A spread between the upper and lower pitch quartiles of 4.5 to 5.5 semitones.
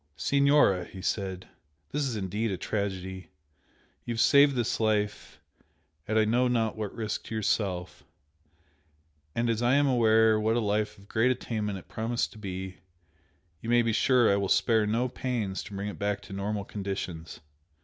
No: average, 3.0 semitones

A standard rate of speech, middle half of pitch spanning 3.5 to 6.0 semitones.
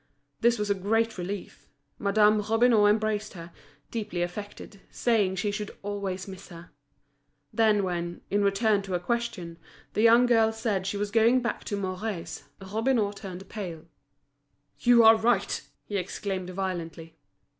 No: average, 145 wpm; average, 3.0 semitones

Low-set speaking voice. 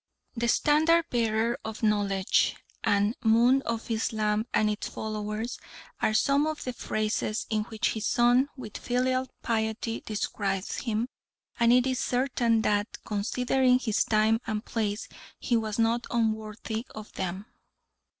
No: high, 225 Hz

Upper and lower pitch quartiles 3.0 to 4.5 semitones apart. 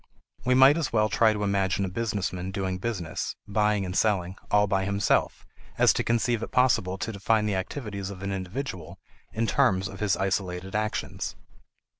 No: narrow, 2.6 semitones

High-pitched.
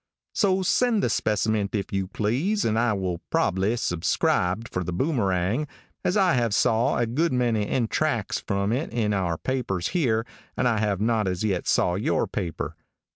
No: low, 110 Hz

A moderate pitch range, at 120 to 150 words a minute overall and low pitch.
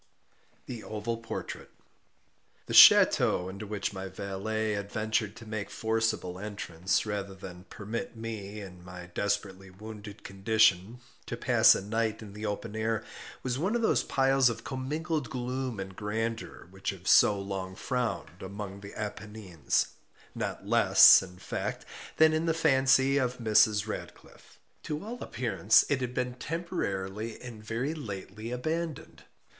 Yes: average, 3.9 semitones; average, 145 wpm; low, 110 Hz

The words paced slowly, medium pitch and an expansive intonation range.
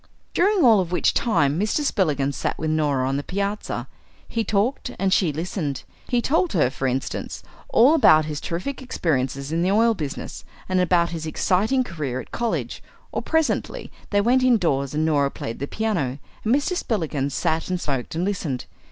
No: average, 180 wpm; medium, 175 Hz; wide, 7.5 semitones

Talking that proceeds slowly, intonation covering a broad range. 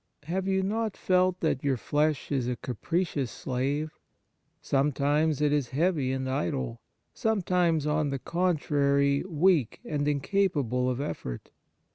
No: slow, 130 wpm; average, 4.4 semitones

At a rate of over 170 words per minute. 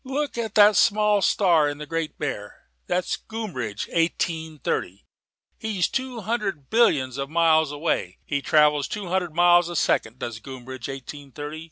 No: average, 160 wpm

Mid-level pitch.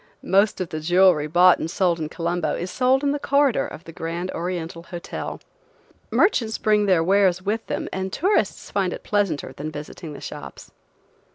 Yes: medium, 180 Hz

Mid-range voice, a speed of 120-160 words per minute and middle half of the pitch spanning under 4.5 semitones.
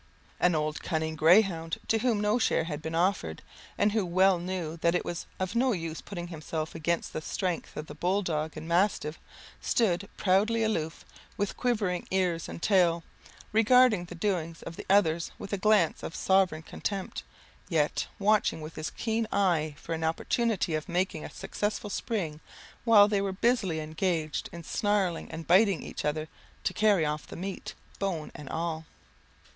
No: medium, 175 Hz; average, 175 wpm; average, 4.1 semitones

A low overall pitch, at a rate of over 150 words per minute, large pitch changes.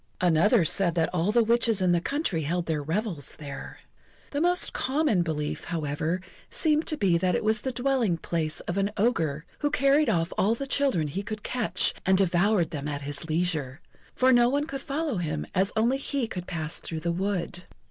No: medium, 185 Hz; average, 200 wpm; wide, 6.8 semitones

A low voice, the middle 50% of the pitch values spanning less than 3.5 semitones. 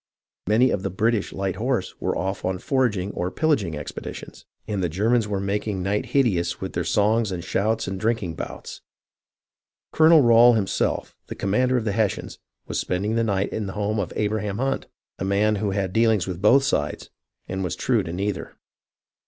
Yes: low, 105 Hz; average, 3.1 semitones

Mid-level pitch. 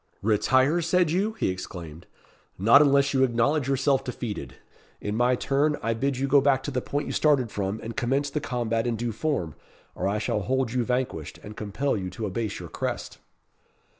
No: low, 125 Hz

